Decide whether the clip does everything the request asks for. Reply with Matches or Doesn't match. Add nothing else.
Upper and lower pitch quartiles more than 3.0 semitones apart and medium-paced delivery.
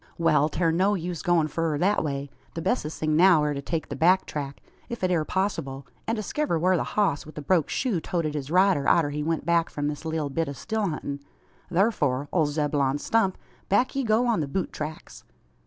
Doesn't match